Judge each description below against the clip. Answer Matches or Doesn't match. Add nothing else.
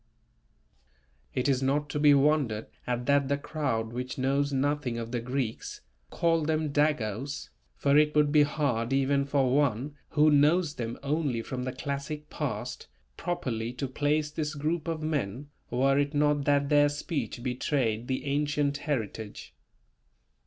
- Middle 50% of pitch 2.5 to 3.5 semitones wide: Matches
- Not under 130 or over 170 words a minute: Matches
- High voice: Doesn't match